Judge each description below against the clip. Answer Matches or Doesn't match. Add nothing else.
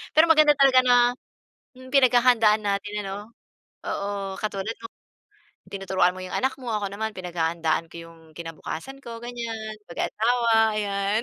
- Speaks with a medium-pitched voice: Doesn't match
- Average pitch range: Matches